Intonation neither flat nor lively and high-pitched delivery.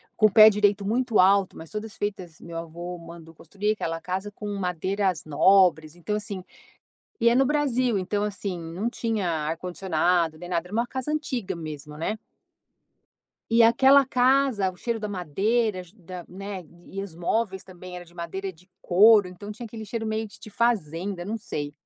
Yes: average, 3.9 semitones; high, 195 Hz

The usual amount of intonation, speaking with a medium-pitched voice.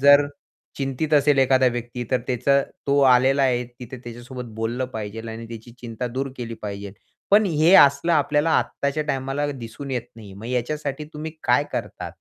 No: average, 3.0 semitones; low, 130 Hz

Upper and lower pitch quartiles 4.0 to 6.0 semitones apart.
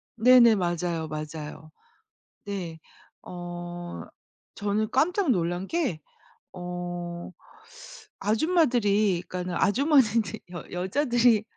Yes: average, 5.2 semitones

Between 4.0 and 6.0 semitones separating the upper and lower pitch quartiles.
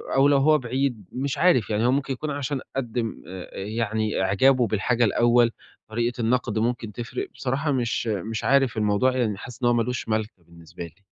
No: average, 3.3 semitones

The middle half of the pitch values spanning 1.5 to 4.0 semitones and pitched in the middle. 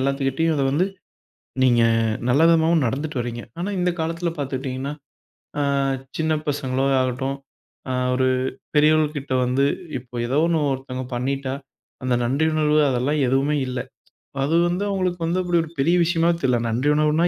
Yes: average, 3.7 semitones; medium, 145 Hz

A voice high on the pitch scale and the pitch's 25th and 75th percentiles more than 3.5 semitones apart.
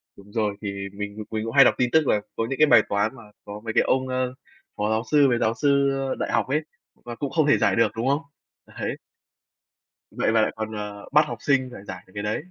No: low, 115 Hz; average, 4.3 semitones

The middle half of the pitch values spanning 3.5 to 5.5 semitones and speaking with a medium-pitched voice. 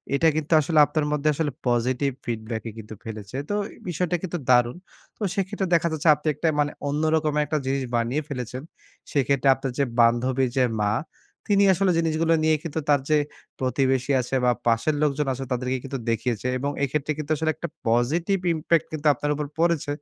Yes: average, 3.9 semitones; medium, 145 Hz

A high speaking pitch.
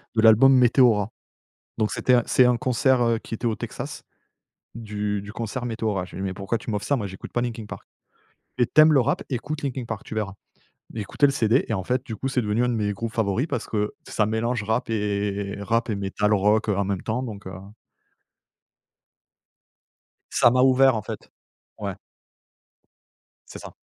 No: low, 110 Hz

